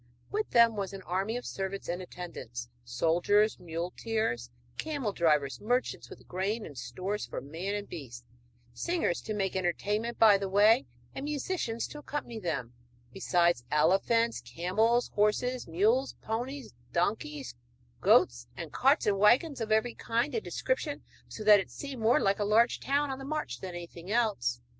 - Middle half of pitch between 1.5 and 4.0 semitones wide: No, average, 5.3 semitones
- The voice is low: No, high, 205 Hz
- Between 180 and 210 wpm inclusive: No, average, 160 wpm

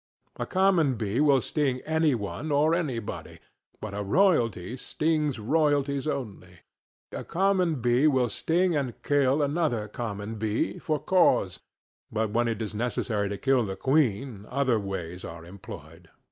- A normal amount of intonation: No, wide, 6.5 semitones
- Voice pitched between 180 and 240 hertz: No, low, 125 Hz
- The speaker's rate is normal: Yes, average, 145 wpm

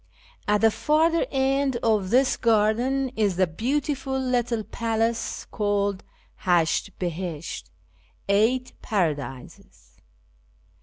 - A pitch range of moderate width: Yes, average, 4.9 semitones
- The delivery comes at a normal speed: No, slow, 100 wpm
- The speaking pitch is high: Yes, high, 225 Hz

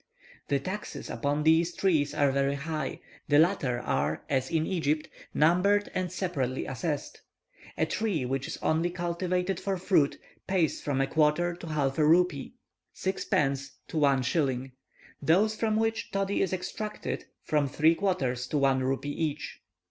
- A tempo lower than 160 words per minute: Yes, average, 150 wpm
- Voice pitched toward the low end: No, medium, 155 Hz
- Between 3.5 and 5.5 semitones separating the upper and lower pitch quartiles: Yes, average, 4.6 semitones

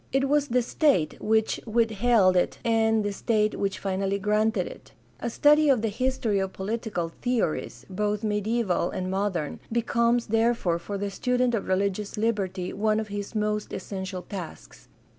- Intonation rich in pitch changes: No, average, 3.2 semitones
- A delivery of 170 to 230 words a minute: No, average, 160 wpm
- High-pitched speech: Yes, high, 210 Hz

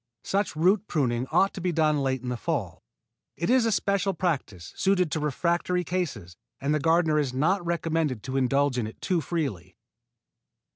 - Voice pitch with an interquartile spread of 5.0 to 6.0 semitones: Yes, wide, 5.4 semitones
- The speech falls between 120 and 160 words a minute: No, average, 180 wpm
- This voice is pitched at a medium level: Yes, medium, 155 Hz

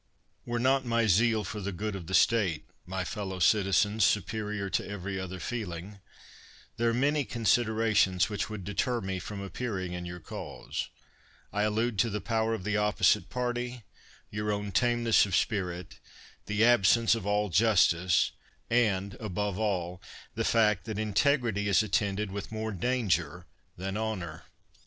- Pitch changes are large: No, average, 3.1 semitones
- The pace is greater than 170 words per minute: No, average, 155 wpm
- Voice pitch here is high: No, low, 105 Hz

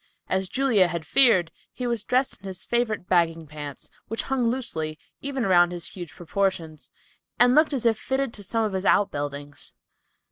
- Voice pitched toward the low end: No, high, 195 Hz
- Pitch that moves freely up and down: Yes, wide, 6.3 semitones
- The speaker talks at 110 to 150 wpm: No, average, 175 wpm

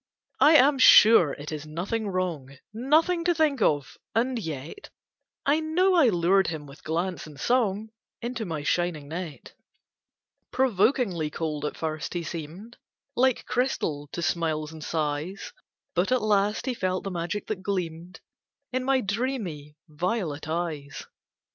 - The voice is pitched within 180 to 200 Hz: Yes, medium, 185 Hz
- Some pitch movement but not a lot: No, wide, 7.3 semitones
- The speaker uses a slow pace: No, average, 145 wpm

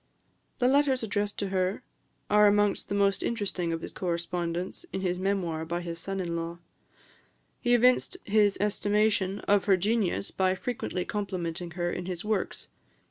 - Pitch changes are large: No, average, 2.9 semitones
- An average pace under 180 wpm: Yes, average, 160 wpm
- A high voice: Yes, high, 195 Hz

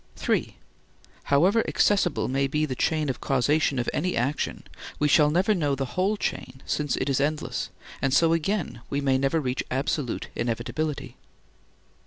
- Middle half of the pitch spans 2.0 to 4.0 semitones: Yes, average, 3.3 semitones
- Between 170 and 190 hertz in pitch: No, medium, 145 Hz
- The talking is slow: No, average, 155 wpm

